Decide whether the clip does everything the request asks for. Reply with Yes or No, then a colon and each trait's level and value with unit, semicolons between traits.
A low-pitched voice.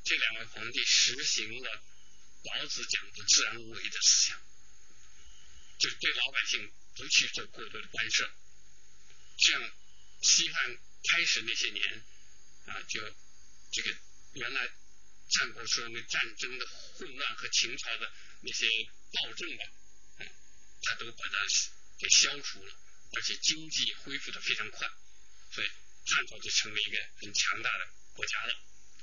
Yes: very low, 85 Hz